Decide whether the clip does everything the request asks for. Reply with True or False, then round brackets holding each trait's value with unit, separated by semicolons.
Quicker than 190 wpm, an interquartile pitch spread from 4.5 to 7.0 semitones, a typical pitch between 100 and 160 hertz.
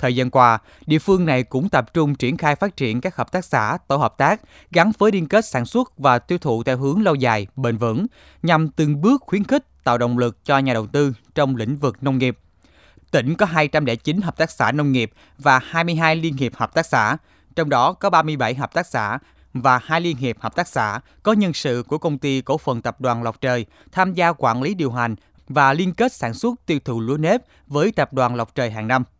True (235 wpm; 5.1 semitones; 140 Hz)